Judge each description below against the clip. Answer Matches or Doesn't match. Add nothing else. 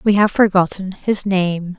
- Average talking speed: Matches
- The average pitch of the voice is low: Doesn't match